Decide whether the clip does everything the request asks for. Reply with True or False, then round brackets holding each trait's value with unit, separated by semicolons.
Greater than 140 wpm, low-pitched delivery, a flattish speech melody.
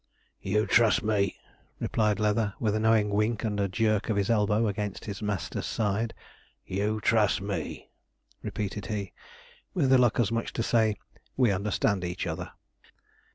True (160 wpm; 105 Hz; 1.8 semitones)